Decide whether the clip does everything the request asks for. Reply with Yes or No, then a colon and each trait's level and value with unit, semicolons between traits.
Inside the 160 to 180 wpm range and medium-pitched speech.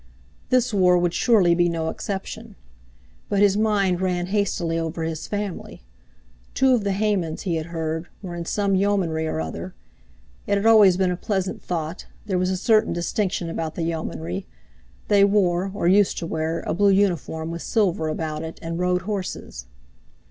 Yes: average, 170 wpm; medium, 180 Hz